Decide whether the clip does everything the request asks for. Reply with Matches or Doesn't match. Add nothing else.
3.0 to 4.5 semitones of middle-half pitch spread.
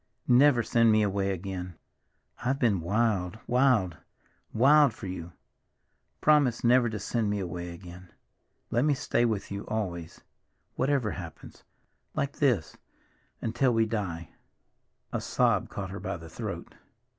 Doesn't match